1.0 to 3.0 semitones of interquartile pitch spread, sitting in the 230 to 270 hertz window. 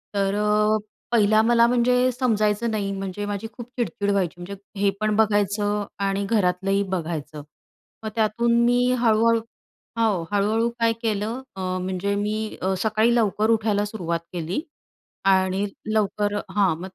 No: narrow, 2.4 semitones; high, 210 Hz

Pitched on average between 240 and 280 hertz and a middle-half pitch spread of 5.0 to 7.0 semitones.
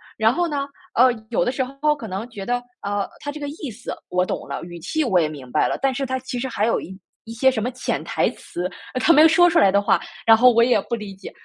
Yes: high, 245 Hz; average, 5.3 semitones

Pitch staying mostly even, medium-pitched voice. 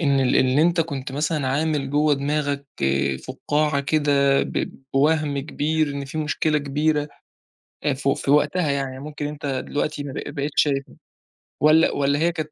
Yes: narrow, 1.7 semitones; medium, 145 Hz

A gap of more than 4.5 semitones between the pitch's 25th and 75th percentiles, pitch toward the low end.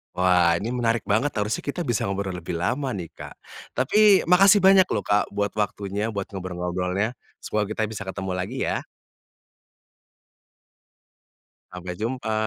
Yes: average, 5.1 semitones; low, 105 Hz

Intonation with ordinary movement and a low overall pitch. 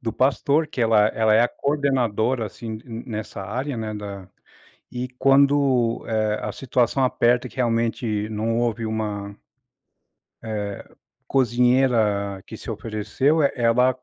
Yes: average, 3.0 semitones; low, 115 Hz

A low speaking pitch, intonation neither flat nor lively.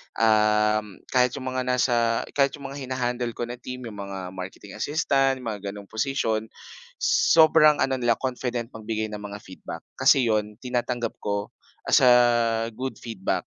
Yes: low, 120 Hz; average, 3.3 semitones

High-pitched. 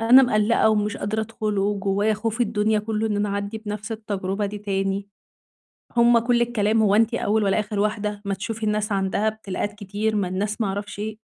Yes: high, 210 Hz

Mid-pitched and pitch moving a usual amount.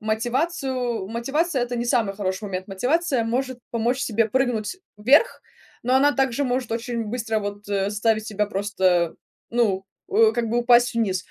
No: high, 230 Hz; average, 3.3 semitones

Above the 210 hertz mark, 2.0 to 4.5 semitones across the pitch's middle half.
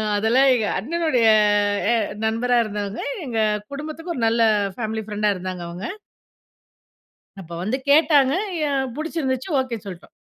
No: high, 240 Hz; average, 4.9 semitones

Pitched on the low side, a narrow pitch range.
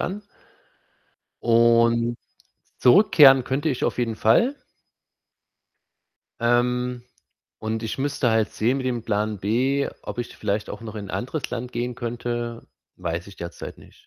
Yes: low, 120 Hz; narrow, 2.2 semitones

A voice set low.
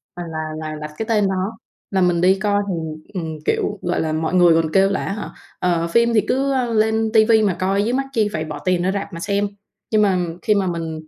No: high, 190 Hz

